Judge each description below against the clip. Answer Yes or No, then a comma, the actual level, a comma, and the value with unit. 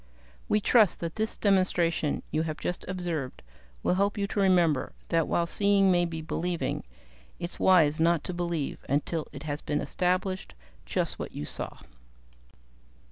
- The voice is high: No, medium, 170 Hz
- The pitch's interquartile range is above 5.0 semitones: No, average, 3.0 semitones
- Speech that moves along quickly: No, average, 155 wpm